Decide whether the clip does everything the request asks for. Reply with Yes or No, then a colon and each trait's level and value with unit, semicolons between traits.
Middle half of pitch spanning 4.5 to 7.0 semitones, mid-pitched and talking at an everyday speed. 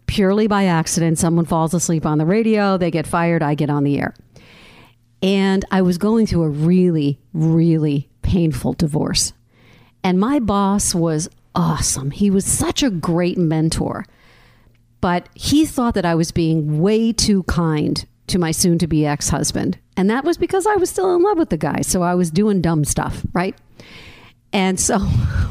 Yes: average, 4.9 semitones; medium, 170 Hz; average, 180 wpm